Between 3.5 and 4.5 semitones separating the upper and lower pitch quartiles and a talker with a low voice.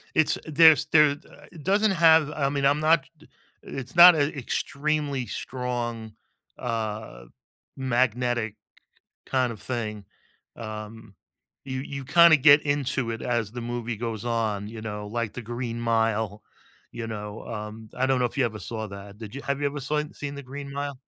Yes: average, 4.2 semitones; low, 125 Hz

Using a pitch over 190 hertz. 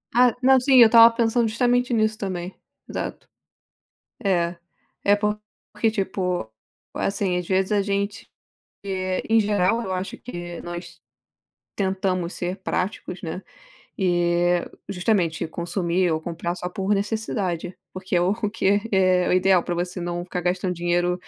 No: medium, 185 Hz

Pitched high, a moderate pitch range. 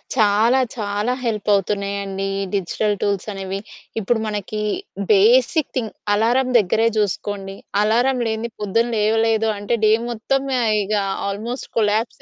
No: high, 215 Hz; narrow, 2.3 semitones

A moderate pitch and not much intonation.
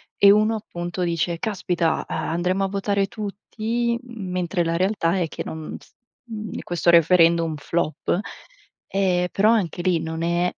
No: medium, 180 Hz; average, 3.1 semitones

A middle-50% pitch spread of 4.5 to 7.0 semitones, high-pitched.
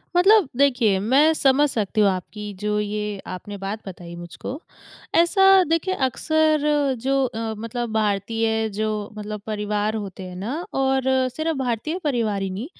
Yes: average, 4.9 semitones; high, 220 Hz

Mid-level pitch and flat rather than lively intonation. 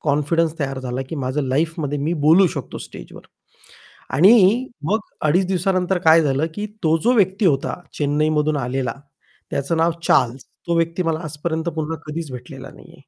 No: medium, 160 Hz; average, 3.4 semitones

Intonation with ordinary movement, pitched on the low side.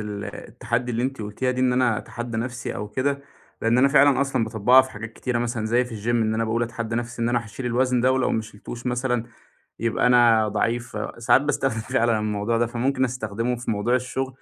No: narrow, 2.2 semitones; low, 120 Hz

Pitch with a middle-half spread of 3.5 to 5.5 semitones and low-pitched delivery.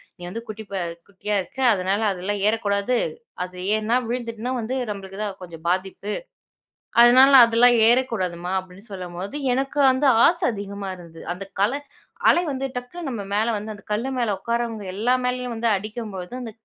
No: average, 4.0 semitones; high, 215 Hz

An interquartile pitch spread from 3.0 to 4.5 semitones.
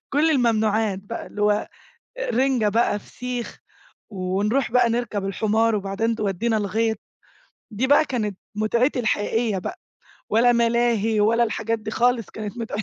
No: narrow, 2.4 semitones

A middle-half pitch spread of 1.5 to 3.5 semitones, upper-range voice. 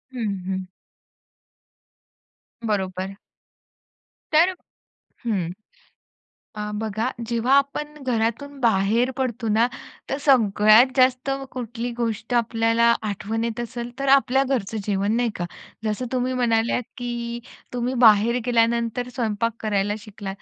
Yes: narrow, 2.6 semitones; high, 230 Hz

